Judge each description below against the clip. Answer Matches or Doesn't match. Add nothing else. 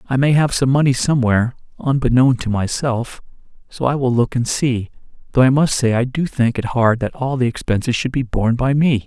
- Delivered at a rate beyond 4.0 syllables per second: Matches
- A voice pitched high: Doesn't match